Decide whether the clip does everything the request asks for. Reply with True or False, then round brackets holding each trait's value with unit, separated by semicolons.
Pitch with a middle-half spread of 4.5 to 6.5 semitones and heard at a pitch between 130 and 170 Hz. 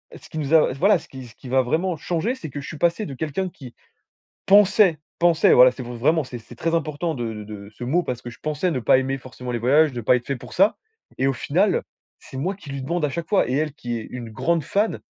True (5.2 semitones; 140 Hz)